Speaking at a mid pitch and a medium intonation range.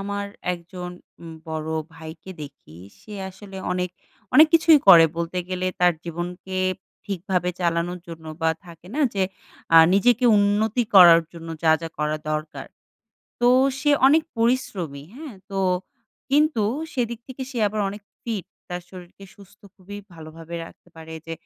Yes: medium, 180 Hz; average, 4.1 semitones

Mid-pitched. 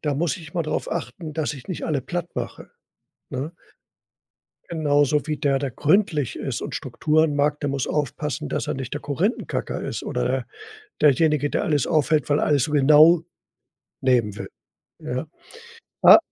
Yes: medium, 150 Hz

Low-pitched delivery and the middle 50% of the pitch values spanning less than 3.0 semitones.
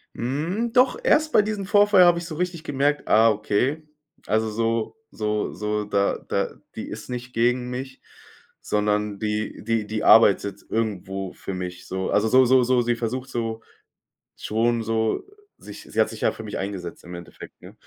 No: low, 115 Hz; average, 4.0 semitones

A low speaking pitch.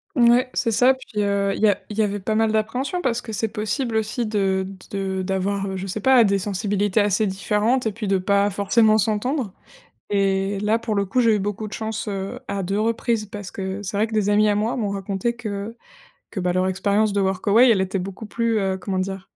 No: high, 205 Hz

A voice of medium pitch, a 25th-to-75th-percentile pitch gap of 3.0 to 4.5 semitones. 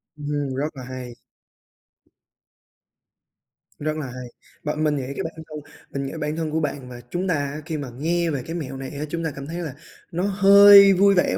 Yes: medium, 150 Hz; average, 3.4 semitones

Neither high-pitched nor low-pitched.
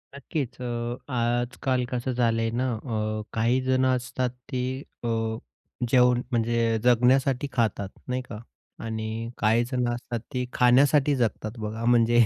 No: low, 120 Hz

